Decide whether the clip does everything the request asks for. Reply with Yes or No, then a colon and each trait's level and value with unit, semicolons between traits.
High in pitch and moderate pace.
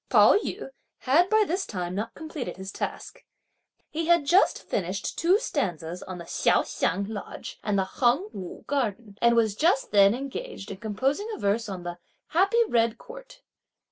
Yes: high, 235 Hz; average, 170 wpm